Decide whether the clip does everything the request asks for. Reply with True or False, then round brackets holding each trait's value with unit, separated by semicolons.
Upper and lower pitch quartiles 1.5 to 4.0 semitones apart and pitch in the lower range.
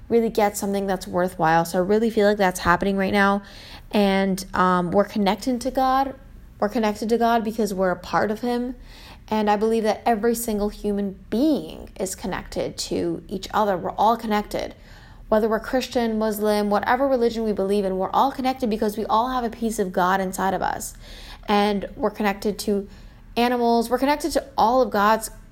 False (2.9 semitones; 210 Hz)